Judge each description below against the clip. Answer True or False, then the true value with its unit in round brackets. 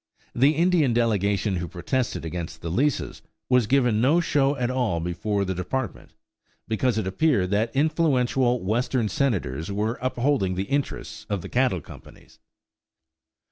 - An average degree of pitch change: False (5.7 semitones)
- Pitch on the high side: False (115 Hz)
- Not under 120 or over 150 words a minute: True (140 wpm)